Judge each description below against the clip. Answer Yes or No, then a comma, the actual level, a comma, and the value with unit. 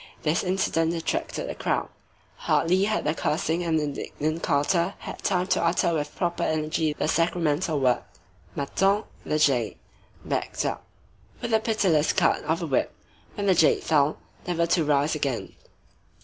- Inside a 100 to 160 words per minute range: Yes, average, 155 wpm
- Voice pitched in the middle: Yes, medium, 165 Hz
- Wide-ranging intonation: No, average, 2.9 semitones